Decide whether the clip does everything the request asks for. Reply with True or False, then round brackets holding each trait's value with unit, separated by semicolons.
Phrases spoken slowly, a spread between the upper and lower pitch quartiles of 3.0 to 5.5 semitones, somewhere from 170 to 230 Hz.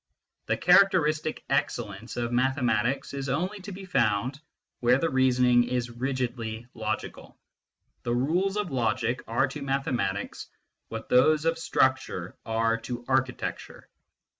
False (125 wpm; 3.8 semitones; 130 Hz)